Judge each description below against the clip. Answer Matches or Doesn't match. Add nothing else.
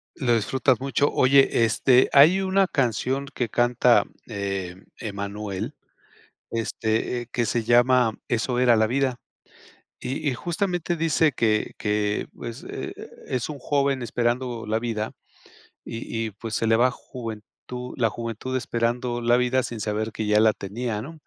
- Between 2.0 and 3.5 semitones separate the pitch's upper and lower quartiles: Matches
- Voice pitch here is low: Matches